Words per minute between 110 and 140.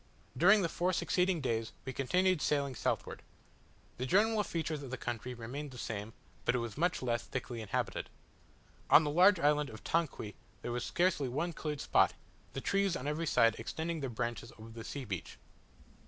No: average, 185 wpm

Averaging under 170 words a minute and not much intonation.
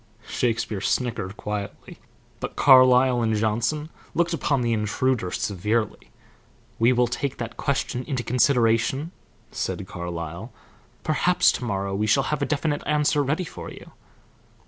No: slow, 135 wpm; average, 4.8 semitones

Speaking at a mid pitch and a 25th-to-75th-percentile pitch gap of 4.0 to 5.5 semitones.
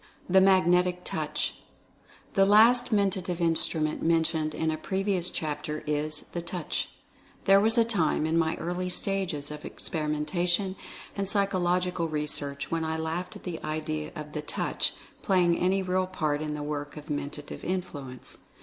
No: medium, 170 Hz; average, 3.5 semitones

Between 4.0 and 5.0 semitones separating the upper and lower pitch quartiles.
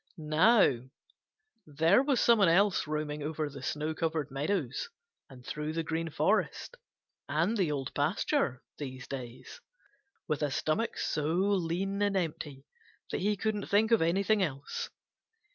No: wide, 5.4 semitones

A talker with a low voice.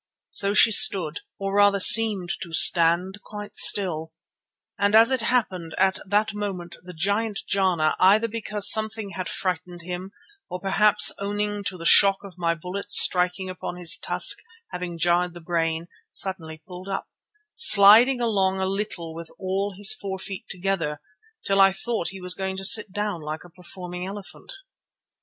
No: high, 190 Hz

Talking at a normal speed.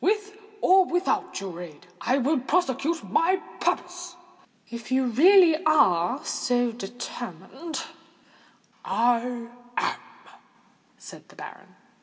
No: slow, 100 wpm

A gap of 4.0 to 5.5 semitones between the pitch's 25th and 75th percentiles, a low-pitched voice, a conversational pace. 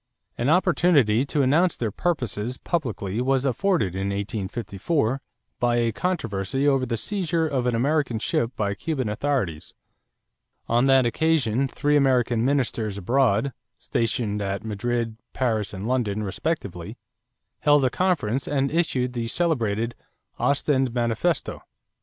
No: average, 4.7 semitones; low, 125 Hz; slow, 130 wpm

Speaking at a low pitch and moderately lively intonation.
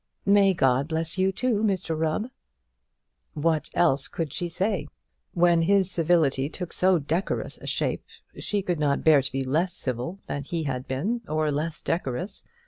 No: medium, 165 Hz; average, 4.6 semitones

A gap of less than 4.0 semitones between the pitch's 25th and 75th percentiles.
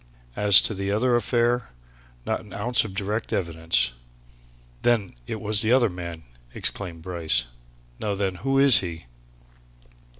No: average, 5.1 semitones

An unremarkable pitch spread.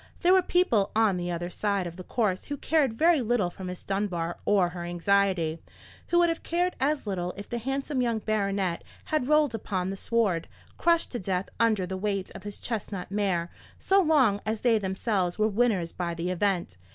Yes: average, 5.0 semitones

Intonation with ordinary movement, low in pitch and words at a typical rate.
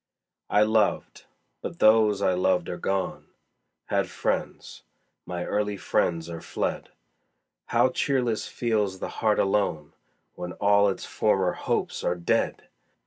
No: average, 3.3 semitones; low, 100 Hz; slow, 130 wpm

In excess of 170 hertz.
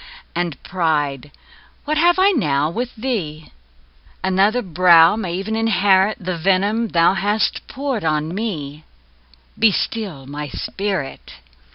Yes: high, 190 Hz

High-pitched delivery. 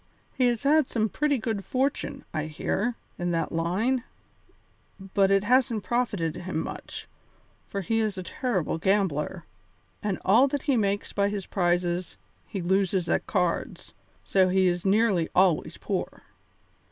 Yes: high, 195 Hz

